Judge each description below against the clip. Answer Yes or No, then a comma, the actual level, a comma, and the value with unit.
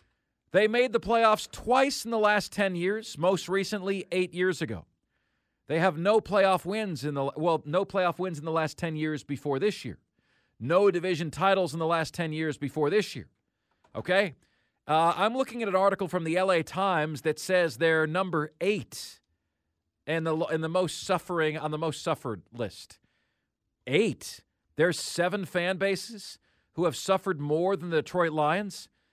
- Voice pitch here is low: No, medium, 175 Hz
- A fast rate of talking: No, average, 175 wpm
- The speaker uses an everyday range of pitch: Yes, average, 4.0 semitones